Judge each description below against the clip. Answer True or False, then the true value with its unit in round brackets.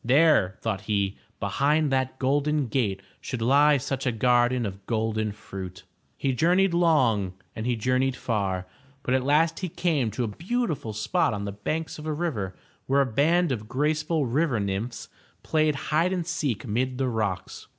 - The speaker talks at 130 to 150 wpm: False (170 wpm)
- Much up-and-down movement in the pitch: True (5.9 semitones)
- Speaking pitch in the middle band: False (130 Hz)